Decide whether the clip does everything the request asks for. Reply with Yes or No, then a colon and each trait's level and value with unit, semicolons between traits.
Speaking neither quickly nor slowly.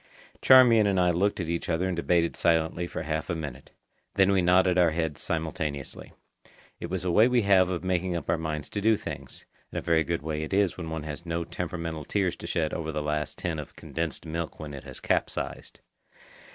No: fast, 220 wpm